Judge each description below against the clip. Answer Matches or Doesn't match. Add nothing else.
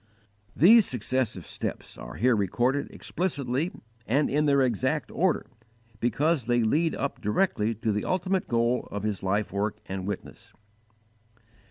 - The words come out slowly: Doesn't match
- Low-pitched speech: Matches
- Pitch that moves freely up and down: Matches